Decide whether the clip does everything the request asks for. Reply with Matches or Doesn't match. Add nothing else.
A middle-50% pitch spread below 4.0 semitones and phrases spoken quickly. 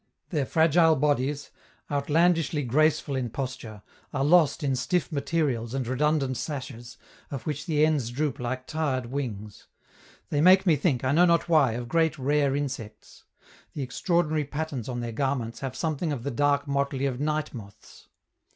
Doesn't match